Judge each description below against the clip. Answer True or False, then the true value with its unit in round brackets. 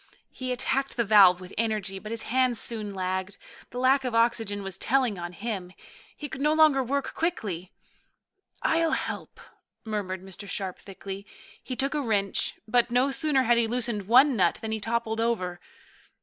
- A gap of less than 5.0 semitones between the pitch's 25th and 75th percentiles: True (4.6 semitones)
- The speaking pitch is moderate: False (225 Hz)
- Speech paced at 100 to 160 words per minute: False (175 wpm)